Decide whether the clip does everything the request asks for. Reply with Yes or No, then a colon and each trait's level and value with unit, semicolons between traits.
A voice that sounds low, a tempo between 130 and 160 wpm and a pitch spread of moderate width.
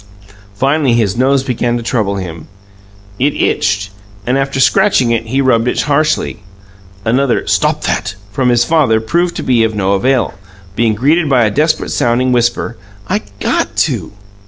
Yes: low, 120 Hz; average, 155 wpm; average, 3.5 semitones